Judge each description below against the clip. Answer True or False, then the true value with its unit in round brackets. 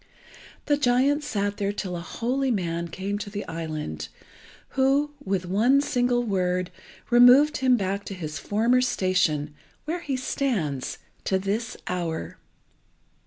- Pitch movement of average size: False (5.9 semitones)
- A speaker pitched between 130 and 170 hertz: False (205 Hz)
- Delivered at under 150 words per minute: True (135 wpm)